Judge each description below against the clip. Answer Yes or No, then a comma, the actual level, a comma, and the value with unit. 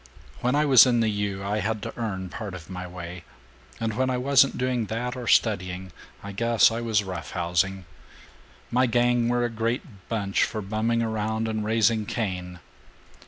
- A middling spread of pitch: Yes, average, 3.5 semitones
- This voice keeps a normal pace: Yes, average, 175 wpm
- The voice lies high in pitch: No, low, 110 Hz